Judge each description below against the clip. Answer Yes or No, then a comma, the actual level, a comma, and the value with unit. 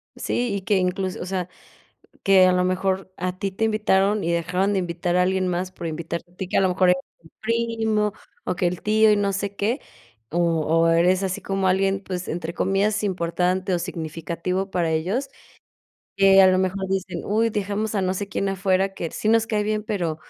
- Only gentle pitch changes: Yes, narrow, 2.0 semitones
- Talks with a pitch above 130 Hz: Yes, high, 190 Hz